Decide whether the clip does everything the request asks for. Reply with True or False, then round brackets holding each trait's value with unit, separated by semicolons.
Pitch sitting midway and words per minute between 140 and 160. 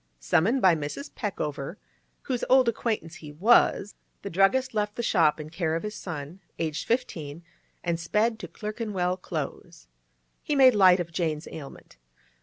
True (180 Hz; 155 wpm)